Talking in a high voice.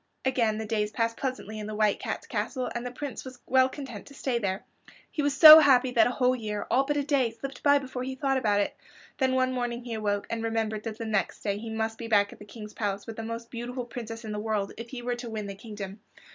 Yes: high, 230 Hz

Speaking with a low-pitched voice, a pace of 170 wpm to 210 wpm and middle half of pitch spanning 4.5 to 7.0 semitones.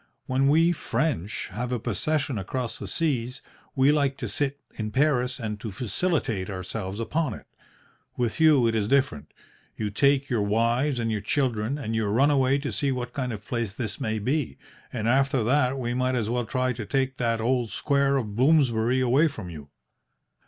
No: low, 125 Hz; average, 190 wpm; average, 3.8 semitones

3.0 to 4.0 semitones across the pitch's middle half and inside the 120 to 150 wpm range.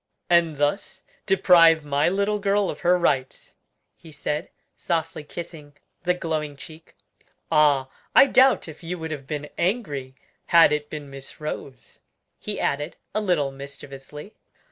Yes: average, 3.4 semitones; average, 145 wpm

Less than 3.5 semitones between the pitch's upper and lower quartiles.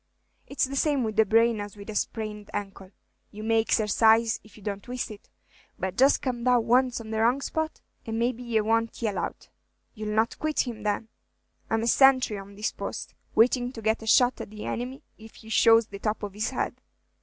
Yes: narrow, 2.4 semitones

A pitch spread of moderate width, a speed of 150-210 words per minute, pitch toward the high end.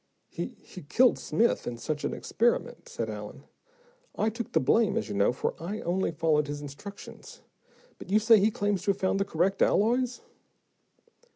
No: wide, 6.1 semitones; average, 180 wpm; high, 195 Hz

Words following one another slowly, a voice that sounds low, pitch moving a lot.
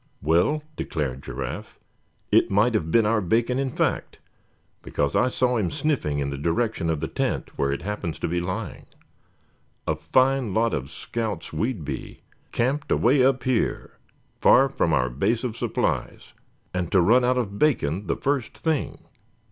No: average, 165 wpm; low, 110 Hz; wide, 7.9 semitones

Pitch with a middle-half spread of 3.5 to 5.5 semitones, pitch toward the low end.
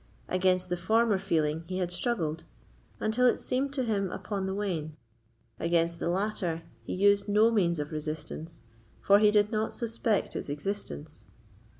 No: average, 4.2 semitones; high, 190 Hz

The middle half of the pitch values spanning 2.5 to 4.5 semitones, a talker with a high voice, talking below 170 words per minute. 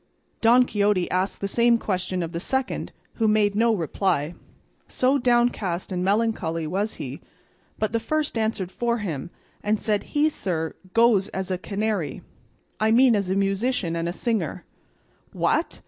Yes: average, 4.0 semitones; high, 205 Hz; average, 160 wpm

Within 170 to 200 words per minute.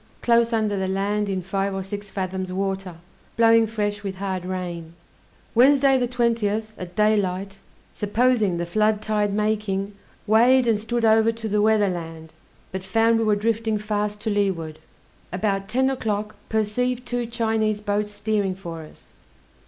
No: average, 155 wpm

